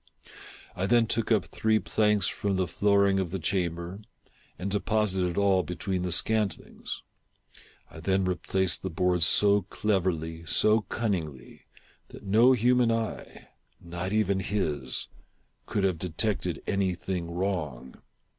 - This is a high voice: No, very low, 95 Hz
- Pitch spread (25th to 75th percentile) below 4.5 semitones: Yes, average, 3.1 semitones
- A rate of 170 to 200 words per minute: No, slow, 135 wpm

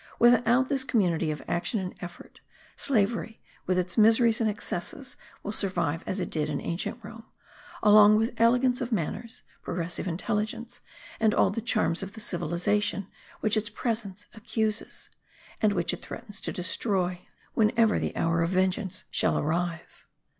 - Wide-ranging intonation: No, average, 4.2 semitones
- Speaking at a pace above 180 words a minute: No, average, 155 wpm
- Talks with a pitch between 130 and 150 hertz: No, high, 210 Hz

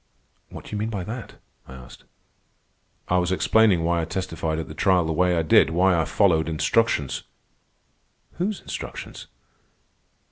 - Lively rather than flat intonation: No, average, 3.7 semitones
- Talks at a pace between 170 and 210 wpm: No, average, 150 wpm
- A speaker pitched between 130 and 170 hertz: No, very low, 90 Hz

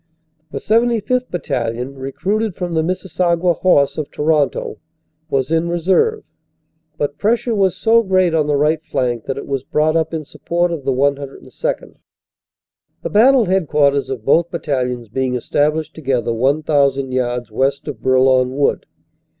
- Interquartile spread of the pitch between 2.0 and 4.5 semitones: No, average, 4.9 semitones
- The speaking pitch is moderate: Yes, medium, 150 Hz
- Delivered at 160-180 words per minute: No, average, 145 wpm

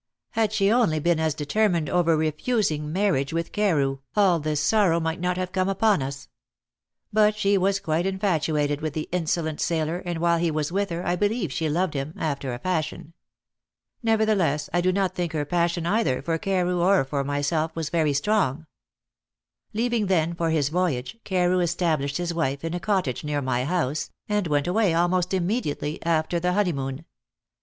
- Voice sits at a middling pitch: Yes, medium, 170 Hz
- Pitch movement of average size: Yes, average, 3.7 semitones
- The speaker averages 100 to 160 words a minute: No, average, 180 wpm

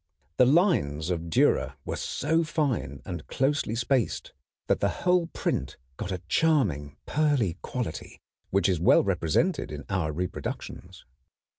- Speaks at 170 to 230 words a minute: No, slow, 135 wpm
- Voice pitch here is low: Yes, low, 100 Hz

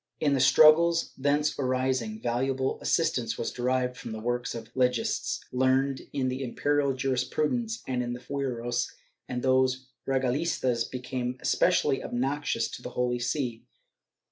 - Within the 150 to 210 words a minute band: No, average, 140 wpm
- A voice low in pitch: Yes, low, 130 Hz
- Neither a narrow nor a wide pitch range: No, narrow, 1.7 semitones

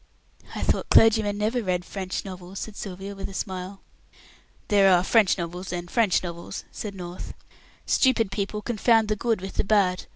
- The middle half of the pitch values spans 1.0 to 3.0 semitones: Yes, average, 2.7 semitones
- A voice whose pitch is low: No, high, 195 Hz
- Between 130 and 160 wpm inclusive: No, average, 170 wpm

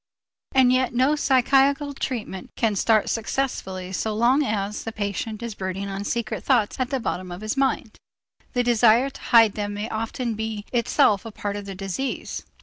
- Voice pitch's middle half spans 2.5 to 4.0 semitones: Yes, average, 3.7 semitones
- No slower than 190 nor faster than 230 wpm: No, average, 180 wpm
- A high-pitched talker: Yes, high, 225 Hz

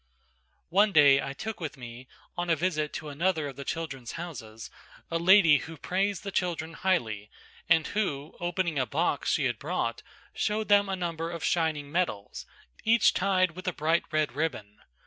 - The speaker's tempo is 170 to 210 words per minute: Yes, average, 175 wpm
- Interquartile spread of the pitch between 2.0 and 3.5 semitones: No, average, 4.3 semitones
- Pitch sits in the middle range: Yes, medium, 165 Hz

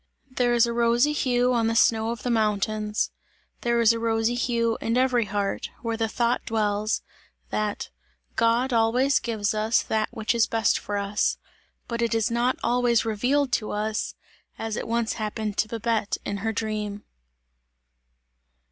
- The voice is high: Yes, high, 225 Hz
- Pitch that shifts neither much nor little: No, narrow, 1.7 semitones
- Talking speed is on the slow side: No, average, 165 wpm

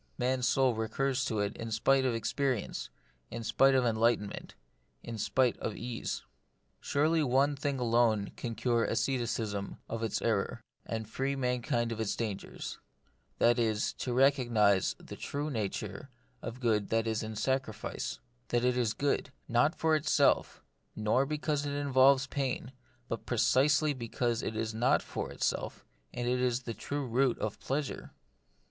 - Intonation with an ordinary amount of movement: Yes, average, 3.2 semitones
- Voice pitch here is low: Yes, low, 120 Hz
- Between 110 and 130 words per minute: No, average, 160 wpm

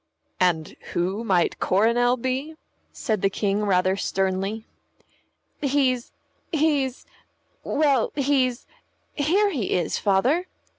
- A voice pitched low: No, high, 235 Hz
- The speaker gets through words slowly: Yes, slow, 100 wpm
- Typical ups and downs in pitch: No, wide, 6.5 semitones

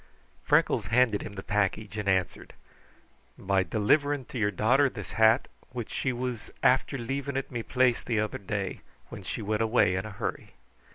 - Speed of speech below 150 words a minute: No, average, 175 wpm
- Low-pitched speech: Yes, low, 110 Hz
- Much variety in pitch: No, average, 3.7 semitones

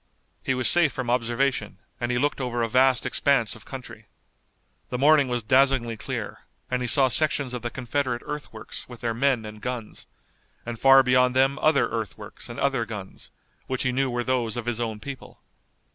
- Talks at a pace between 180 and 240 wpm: Yes, average, 190 wpm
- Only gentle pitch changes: Yes, narrow, 2.2 semitones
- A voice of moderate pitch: No, low, 125 Hz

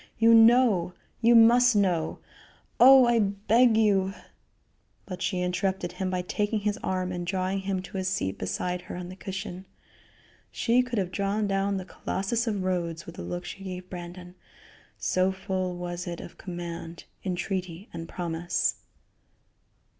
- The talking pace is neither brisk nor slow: Yes, average, 160 wpm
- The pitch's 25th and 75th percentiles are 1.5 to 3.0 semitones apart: Yes, narrow, 2.6 semitones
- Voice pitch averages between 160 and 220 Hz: Yes, high, 190 Hz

